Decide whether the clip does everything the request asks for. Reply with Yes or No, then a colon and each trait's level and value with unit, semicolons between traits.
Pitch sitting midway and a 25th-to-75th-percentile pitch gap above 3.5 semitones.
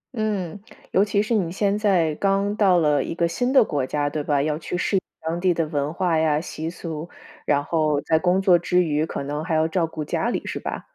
Yes: medium, 170 Hz; average, 3.9 semitones